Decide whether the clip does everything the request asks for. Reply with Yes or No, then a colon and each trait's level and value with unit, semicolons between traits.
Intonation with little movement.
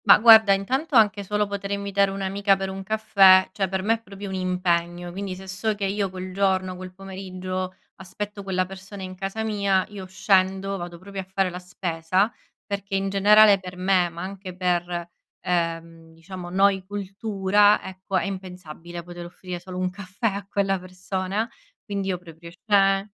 Yes: narrow, 1.5 semitones